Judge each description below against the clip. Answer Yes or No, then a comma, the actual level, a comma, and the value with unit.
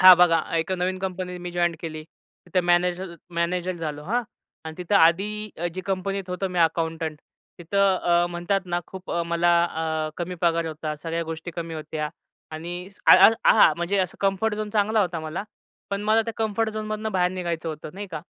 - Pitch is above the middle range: No, medium, 175 Hz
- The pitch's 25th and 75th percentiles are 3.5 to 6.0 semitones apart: No, average, 3.0 semitones